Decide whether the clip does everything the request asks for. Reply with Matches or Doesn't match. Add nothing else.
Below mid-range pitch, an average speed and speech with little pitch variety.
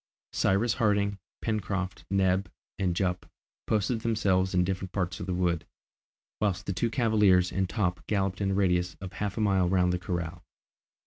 Matches